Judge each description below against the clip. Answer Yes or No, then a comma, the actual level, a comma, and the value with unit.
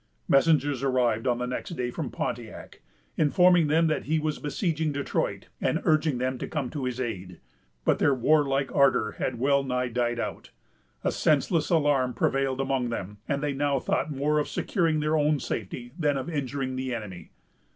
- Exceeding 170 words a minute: Yes, average, 180 wpm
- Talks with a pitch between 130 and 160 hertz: Yes, low, 135 Hz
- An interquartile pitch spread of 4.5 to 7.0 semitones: No, average, 3.3 semitones